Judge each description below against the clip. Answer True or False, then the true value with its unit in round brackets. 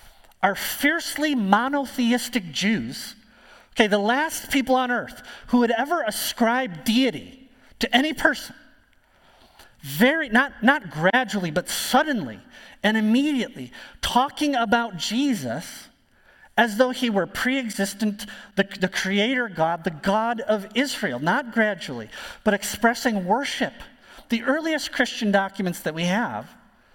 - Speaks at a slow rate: True (120 wpm)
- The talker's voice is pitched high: True (235 Hz)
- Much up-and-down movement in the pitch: False (4.1 semitones)